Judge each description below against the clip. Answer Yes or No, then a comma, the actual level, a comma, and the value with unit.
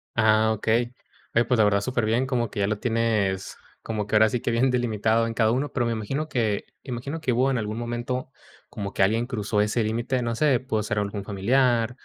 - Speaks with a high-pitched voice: No, low, 115 Hz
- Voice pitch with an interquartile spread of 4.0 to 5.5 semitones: No, narrow, 2.5 semitones